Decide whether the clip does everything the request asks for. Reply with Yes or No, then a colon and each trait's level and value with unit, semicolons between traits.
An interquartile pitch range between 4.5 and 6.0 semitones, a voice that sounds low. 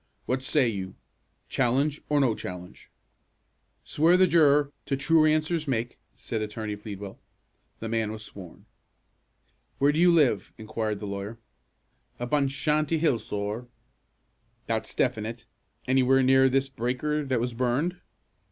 Yes: average, 5.2 semitones; low, 130 Hz